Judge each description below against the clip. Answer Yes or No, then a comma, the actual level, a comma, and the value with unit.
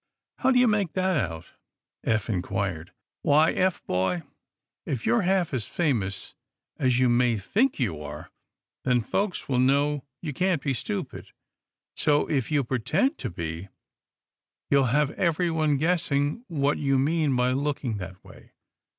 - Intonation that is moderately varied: No, wide, 6.4 semitones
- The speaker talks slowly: No, average, 150 wpm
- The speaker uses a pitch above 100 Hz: Yes, medium, 140 Hz